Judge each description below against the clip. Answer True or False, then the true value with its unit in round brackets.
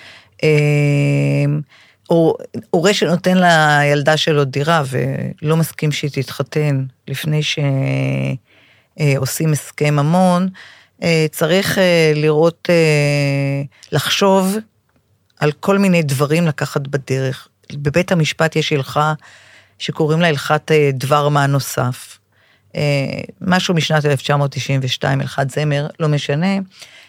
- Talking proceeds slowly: True (95 wpm)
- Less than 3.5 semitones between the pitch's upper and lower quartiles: True (2.7 semitones)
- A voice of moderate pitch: True (150 Hz)